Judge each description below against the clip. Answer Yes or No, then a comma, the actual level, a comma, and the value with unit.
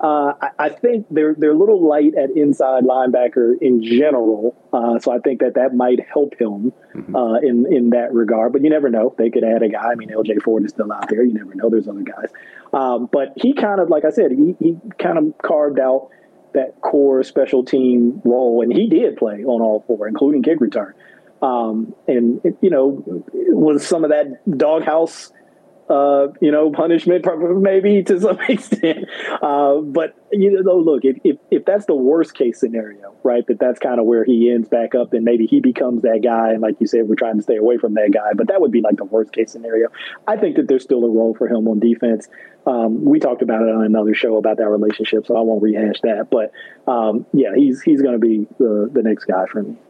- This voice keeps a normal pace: No, fast, 230 wpm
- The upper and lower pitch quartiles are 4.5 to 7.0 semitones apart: Yes, wide, 5.5 semitones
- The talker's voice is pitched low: Yes, low, 125 Hz